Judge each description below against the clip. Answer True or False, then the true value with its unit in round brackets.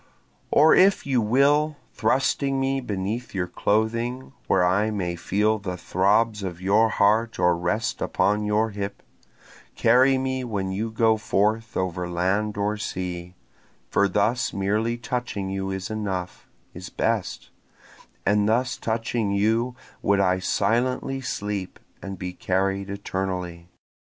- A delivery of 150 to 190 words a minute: False (135 wpm)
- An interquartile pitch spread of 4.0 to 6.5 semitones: False (3.3 semitones)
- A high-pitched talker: False (105 Hz)